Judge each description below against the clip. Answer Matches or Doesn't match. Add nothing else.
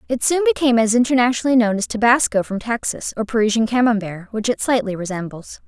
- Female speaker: Matches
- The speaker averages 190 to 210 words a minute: Doesn't match